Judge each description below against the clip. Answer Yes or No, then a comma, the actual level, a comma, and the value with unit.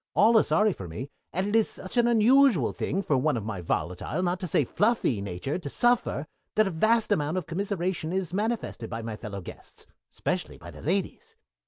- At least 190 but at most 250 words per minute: Yes, fast, 205 wpm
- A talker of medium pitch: Yes, medium, 180 Hz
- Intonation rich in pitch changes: Yes, wide, 8.7 semitones